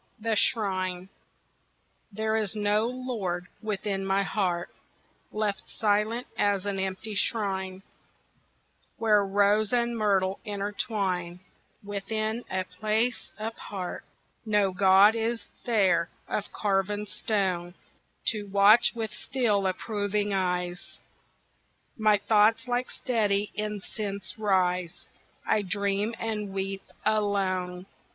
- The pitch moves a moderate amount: No, narrow, 2.1 semitones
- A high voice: Yes, high, 205 Hz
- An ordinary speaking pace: No, slow, 100 wpm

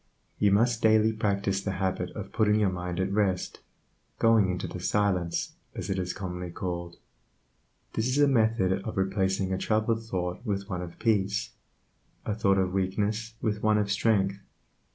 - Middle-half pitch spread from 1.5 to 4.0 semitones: Yes, narrow, 2.6 semitones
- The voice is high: No, low, 100 Hz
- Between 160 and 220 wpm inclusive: Yes, average, 170 wpm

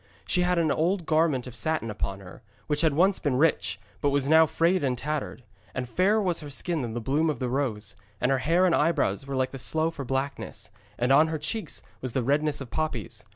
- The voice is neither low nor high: Yes, medium, 145 Hz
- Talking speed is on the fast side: Yes, fast, 230 wpm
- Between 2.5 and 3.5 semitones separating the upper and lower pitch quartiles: No, average, 4.1 semitones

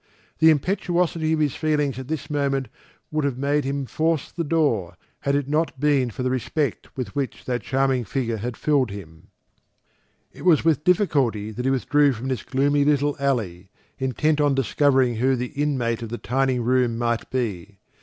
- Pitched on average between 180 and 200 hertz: No, low, 135 Hz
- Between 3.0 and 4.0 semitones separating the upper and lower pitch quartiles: Yes, average, 3.3 semitones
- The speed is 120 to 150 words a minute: No, average, 175 wpm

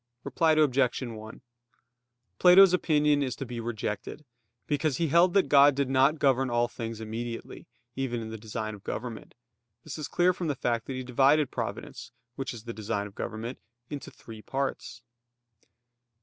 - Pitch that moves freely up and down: No, average, 4.3 semitones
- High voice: No, low, 130 Hz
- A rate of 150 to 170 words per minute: Yes, average, 165 wpm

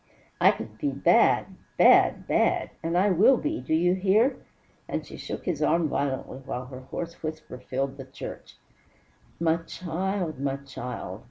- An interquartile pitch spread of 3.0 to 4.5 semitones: No, average, 5.0 semitones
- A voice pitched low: No, medium, 155 Hz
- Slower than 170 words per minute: Yes, average, 160 wpm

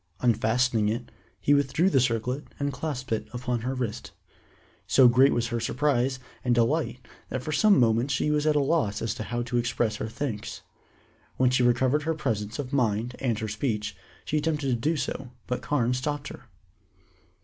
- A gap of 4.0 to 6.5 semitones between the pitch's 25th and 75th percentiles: No, average, 3.5 semitones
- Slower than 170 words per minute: No, average, 180 wpm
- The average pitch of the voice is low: Yes, low, 125 Hz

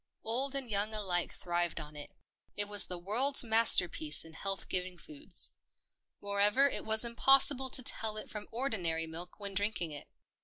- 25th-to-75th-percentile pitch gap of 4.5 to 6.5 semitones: Yes, average, 5.0 semitones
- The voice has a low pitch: No, high, 205 Hz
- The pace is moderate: Yes, average, 180 wpm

